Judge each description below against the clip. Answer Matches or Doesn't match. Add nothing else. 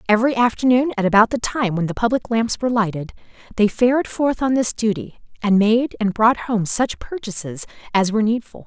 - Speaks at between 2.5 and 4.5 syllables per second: Doesn't match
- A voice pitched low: Doesn't match